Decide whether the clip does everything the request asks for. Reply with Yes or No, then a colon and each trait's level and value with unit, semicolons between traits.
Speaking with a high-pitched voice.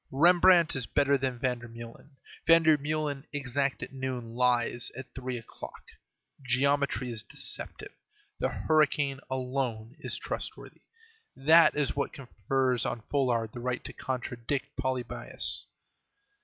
No: low, 130 Hz